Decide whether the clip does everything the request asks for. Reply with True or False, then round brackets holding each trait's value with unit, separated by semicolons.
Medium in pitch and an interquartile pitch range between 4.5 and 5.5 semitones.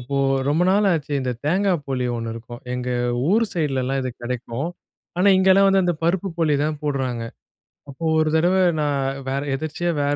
True (150 Hz; 5.2 semitones)